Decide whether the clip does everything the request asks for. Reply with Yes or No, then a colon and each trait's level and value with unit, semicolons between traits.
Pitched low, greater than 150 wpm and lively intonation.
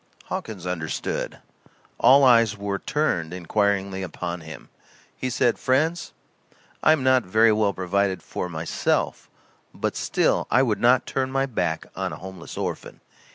No: low, 100 Hz; average, 145 wpm; wide, 6.0 semitones